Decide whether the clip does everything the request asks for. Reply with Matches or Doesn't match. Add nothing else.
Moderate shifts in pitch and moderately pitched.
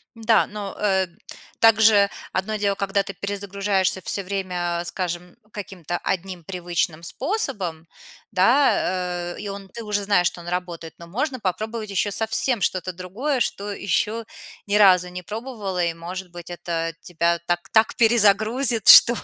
Doesn't match